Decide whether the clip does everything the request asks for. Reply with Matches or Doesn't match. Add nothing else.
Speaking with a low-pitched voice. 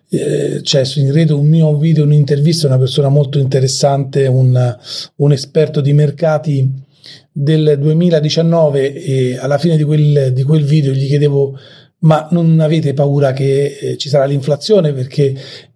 Doesn't match